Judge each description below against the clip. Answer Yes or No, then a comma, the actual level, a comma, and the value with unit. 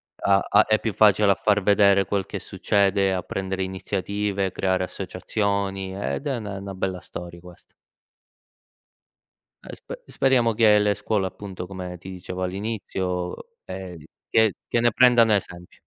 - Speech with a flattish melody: Yes, narrow, 2.0 semitones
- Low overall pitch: Yes, low, 100 Hz